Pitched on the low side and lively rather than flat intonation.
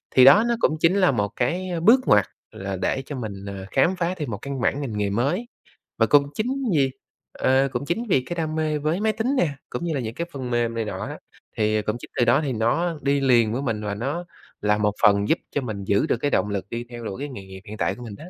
Yes: low, 130 Hz; wide, 6.7 semitones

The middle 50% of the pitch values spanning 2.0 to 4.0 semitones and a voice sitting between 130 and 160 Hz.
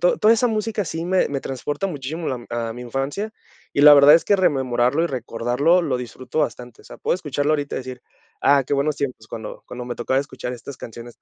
No: average, 4.7 semitones; medium, 140 Hz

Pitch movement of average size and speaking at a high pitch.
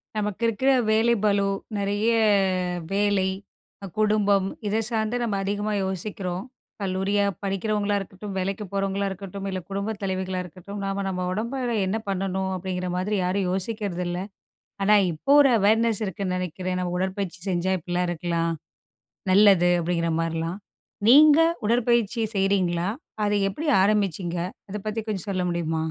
No: narrow, 2.3 semitones; high, 195 Hz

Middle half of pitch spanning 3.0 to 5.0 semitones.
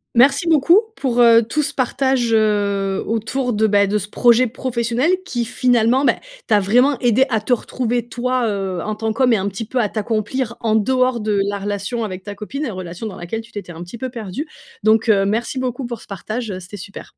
Yes: average, 3.4 semitones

